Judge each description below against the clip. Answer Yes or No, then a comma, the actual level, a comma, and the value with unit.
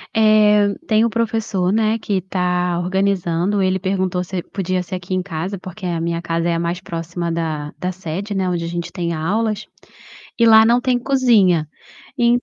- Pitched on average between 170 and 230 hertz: Yes, medium, 185 Hz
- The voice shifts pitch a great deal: No, average, 3.7 semitones